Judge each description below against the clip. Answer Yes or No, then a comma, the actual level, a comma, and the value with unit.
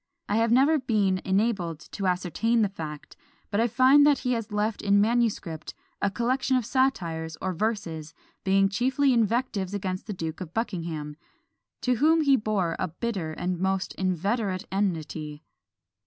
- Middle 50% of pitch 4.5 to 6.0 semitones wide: Yes, average, 4.9 semitones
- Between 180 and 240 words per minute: No, average, 155 wpm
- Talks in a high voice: Yes, high, 200 Hz